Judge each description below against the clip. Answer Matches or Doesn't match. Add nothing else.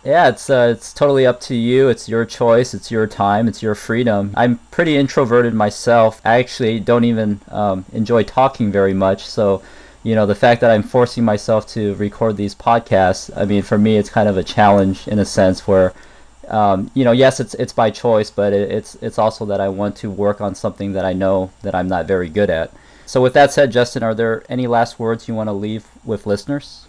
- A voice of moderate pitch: Doesn't match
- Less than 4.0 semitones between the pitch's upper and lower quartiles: Matches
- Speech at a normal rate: Doesn't match